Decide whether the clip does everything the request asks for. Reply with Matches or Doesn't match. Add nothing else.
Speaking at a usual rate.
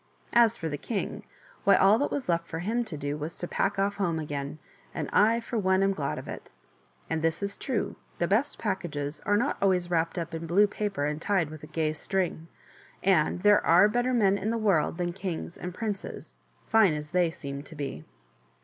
Doesn't match